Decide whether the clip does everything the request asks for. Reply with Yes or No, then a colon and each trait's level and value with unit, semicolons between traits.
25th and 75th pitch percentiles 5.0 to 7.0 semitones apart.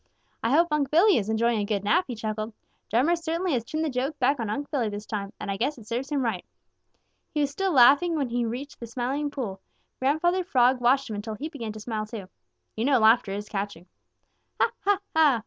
Yes: average, 5.3 semitones